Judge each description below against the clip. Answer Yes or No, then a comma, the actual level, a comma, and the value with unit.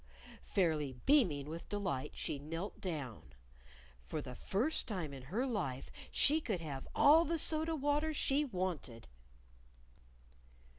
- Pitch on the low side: No, medium, 180 Hz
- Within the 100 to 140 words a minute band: Yes, slow, 135 wpm